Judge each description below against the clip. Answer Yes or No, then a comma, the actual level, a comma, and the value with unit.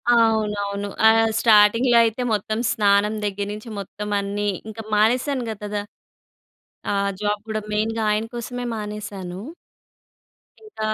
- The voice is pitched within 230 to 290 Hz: No, high, 210 Hz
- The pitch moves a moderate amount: No, narrow, 1.6 semitones